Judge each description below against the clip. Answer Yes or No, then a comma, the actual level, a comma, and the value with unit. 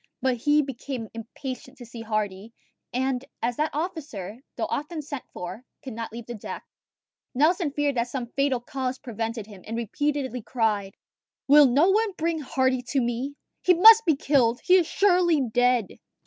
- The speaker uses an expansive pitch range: No, average, 4.3 semitones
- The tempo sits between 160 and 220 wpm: Yes, average, 170 wpm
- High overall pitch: Yes, very high, 260 Hz